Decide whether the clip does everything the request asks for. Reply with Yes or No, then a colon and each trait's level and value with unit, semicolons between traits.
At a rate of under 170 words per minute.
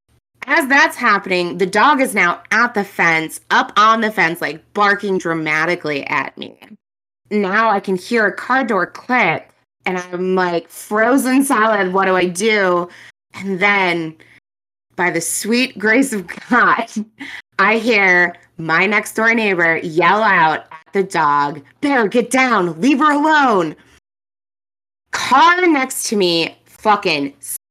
Yes: average, 145 wpm